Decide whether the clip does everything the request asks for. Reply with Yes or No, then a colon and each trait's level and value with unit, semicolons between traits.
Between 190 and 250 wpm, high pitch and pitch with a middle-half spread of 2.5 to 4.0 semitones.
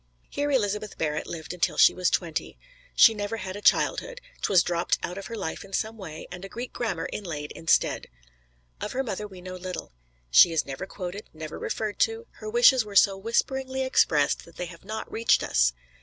No: average, 200 wpm; high, 195 Hz; average, 4.7 semitones